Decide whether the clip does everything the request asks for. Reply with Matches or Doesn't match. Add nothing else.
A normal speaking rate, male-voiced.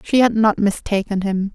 Doesn't match